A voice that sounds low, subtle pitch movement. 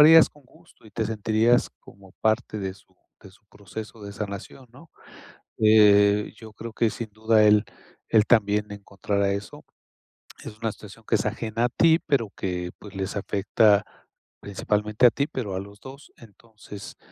Yes: low, 105 Hz; narrow, 2.2 semitones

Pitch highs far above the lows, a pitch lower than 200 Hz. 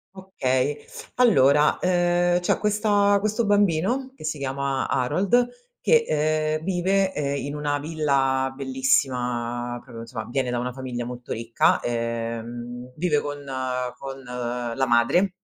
Yes: wide, 6.4 semitones; medium, 140 Hz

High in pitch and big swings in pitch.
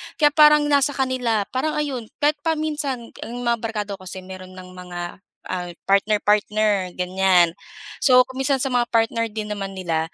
Yes: high, 220 Hz; wide, 6.0 semitones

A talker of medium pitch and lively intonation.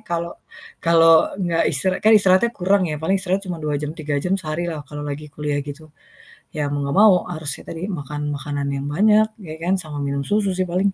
No: medium, 165 Hz; average, 4.1 semitones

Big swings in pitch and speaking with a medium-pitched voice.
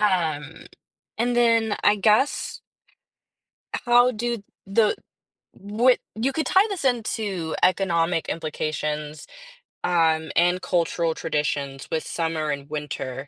Yes: wide, 6.3 semitones; medium, 175 Hz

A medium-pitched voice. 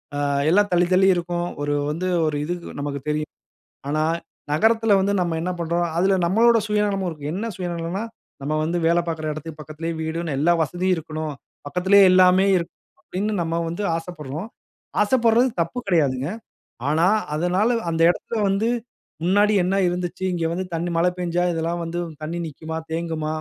Yes: medium, 175 Hz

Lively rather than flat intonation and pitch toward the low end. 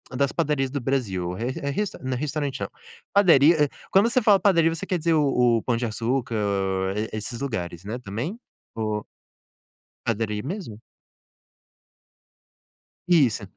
Yes: wide, 6.1 semitones; low, 130 Hz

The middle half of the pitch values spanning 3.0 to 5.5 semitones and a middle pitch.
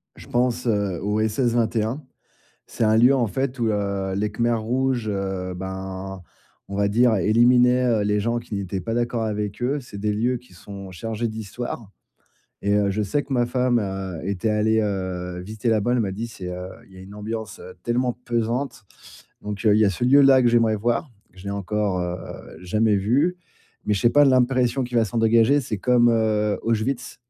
No: average, 3.3 semitones; low, 110 Hz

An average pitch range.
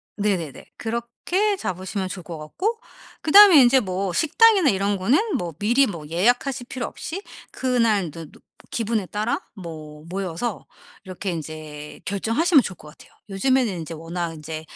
No: wide, 7.2 semitones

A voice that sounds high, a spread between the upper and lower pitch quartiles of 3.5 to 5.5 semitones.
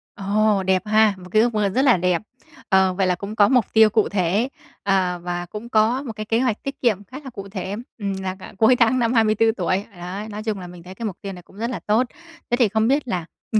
No: high, 210 Hz; average, 3.1 semitones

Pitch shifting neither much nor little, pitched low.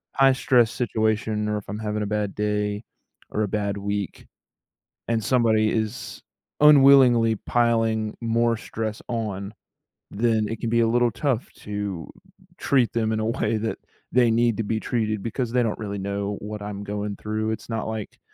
No: narrow, 1.9 semitones; low, 110 Hz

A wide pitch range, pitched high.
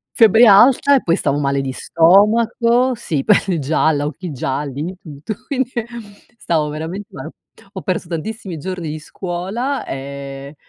No: wide, 7.0 semitones; medium, 175 Hz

